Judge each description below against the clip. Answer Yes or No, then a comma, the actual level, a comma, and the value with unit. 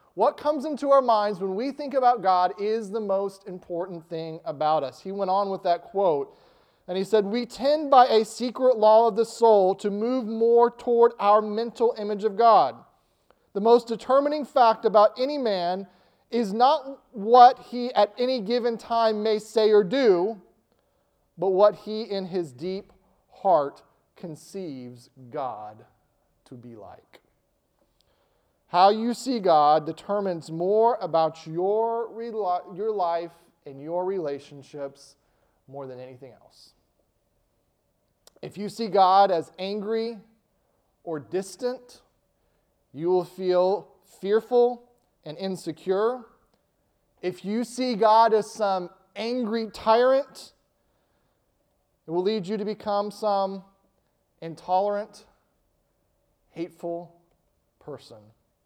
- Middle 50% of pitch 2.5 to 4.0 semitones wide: No, average, 4.8 semitones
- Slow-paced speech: Yes, slow, 130 wpm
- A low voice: No, high, 205 Hz